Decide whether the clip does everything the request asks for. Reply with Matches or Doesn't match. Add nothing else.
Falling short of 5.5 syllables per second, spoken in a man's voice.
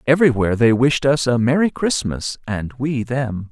Matches